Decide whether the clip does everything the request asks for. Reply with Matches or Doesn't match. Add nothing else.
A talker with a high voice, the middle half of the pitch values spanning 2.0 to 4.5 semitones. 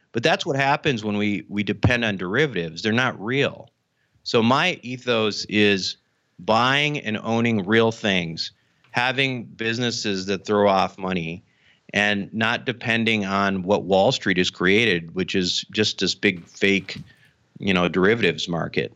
Doesn't match